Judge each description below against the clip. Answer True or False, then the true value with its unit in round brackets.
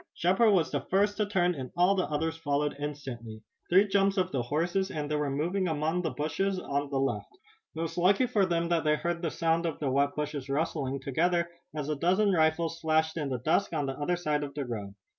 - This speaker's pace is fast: True (235 wpm)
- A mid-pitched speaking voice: True (160 Hz)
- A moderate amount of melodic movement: True (3.7 semitones)